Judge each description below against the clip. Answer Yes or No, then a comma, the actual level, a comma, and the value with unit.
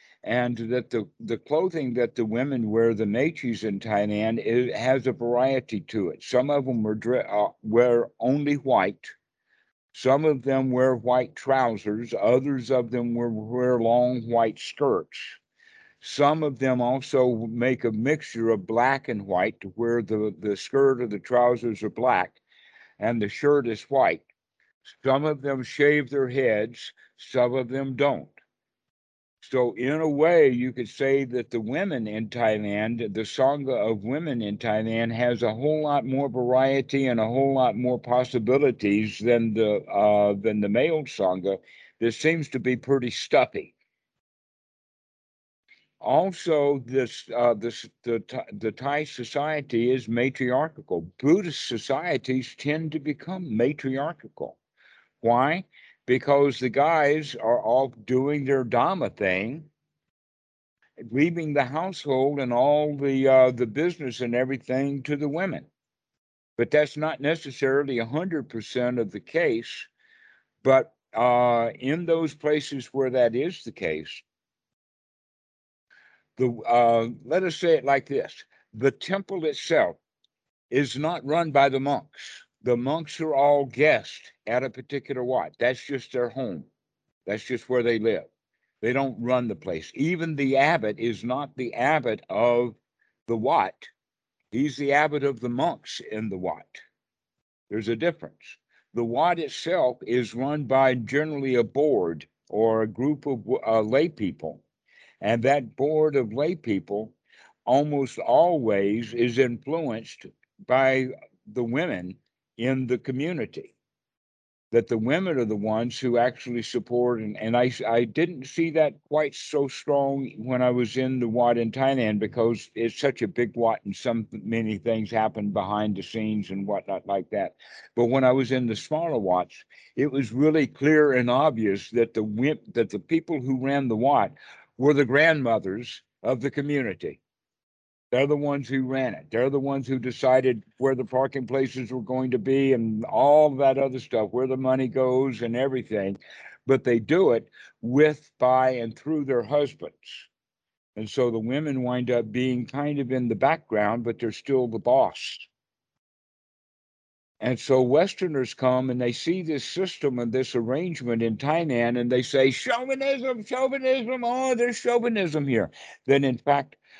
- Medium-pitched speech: No, low, 130 Hz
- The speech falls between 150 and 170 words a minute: Yes, average, 155 wpm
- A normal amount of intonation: Yes, average, 3.3 semitones